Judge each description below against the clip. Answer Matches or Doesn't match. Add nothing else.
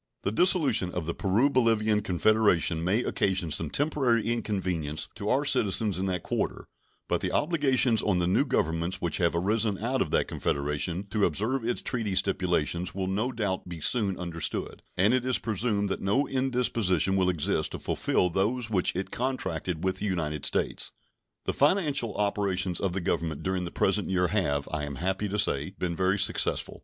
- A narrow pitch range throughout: Doesn't match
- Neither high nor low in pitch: Doesn't match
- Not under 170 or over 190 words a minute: Matches